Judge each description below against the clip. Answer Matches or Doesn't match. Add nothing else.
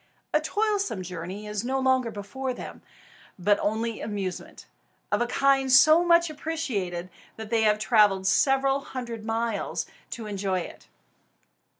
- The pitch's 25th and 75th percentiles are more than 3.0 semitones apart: Matches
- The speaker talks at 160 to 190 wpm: Doesn't match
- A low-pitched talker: Doesn't match